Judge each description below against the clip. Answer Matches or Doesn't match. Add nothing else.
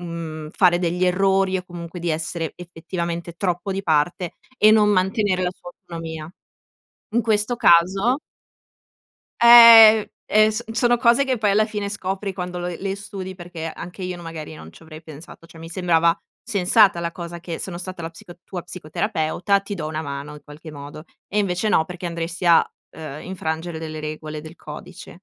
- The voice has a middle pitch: Matches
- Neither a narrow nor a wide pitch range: Matches